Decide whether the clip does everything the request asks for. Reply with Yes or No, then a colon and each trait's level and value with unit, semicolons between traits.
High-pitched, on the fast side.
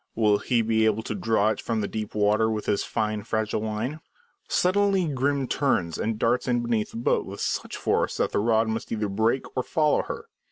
No: low, 110 Hz; fast, 210 wpm